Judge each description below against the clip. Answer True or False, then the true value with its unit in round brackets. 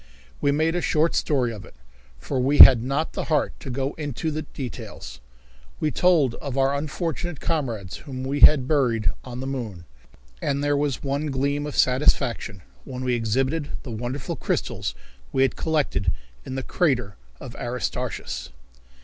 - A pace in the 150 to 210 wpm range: True (160 wpm)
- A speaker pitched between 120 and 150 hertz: True (135 Hz)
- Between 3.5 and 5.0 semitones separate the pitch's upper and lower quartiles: False (3.0 semitones)